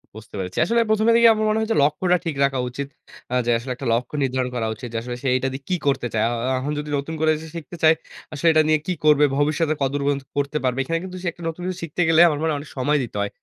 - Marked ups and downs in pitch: No, average, 4.2 semitones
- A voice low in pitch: No, medium, 145 Hz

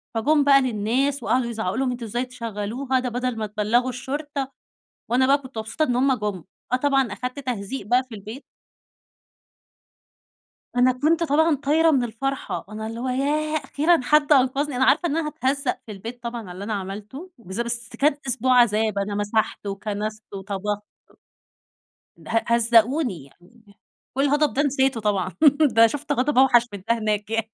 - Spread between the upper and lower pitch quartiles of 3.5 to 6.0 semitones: Yes, average, 4.2 semitones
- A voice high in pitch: Yes, high, 245 Hz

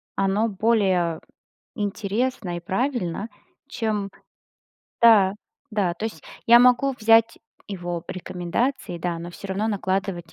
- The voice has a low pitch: No, high, 200 Hz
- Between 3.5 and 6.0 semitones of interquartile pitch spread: Yes, average, 4.3 semitones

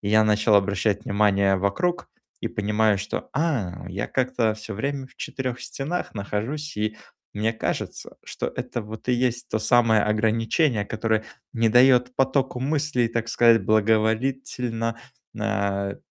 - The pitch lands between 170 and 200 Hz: No, low, 110 Hz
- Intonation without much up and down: No, average, 3.2 semitones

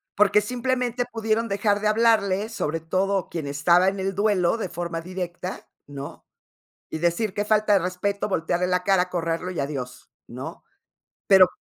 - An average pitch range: Yes, average, 3.4 semitones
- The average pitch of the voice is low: No, medium, 185 Hz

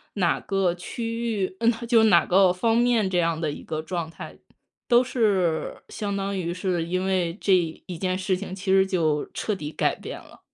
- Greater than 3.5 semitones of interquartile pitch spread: No, average, 3.1 semitones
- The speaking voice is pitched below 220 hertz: Yes, high, 190 Hz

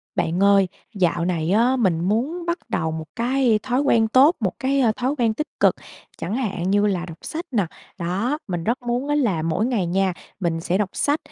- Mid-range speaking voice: No, high, 215 Hz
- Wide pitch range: Yes, wide, 6.3 semitones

